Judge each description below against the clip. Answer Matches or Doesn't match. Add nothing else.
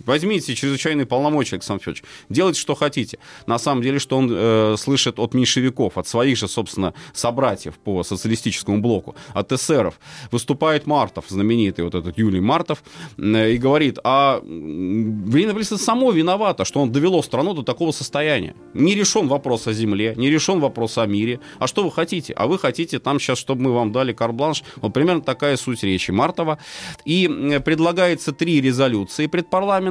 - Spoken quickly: Matches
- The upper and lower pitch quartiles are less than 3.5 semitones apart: Doesn't match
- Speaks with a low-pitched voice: Matches